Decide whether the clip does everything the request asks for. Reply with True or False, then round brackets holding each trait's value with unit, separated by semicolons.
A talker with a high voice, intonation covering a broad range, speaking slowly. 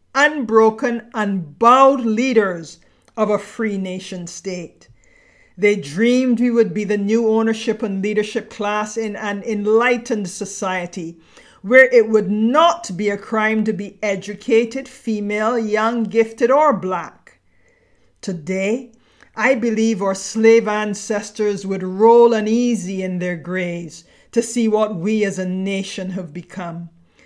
False (215 Hz; 3.0 semitones; 130 wpm)